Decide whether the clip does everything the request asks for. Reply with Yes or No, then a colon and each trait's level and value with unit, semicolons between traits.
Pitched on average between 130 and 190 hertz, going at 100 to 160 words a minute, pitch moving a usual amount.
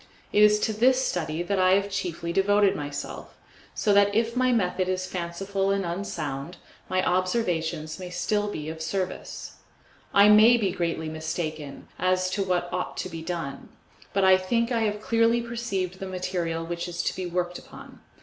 No: medium, 185 Hz; average, 180 wpm; average, 3.1 semitones